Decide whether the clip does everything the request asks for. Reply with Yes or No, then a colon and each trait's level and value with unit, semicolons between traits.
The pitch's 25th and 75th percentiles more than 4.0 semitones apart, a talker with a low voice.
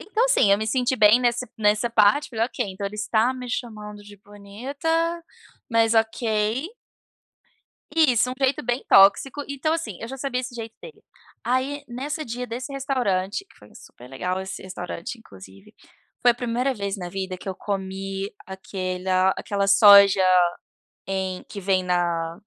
No: average, 4.5 semitones; high, 215 Hz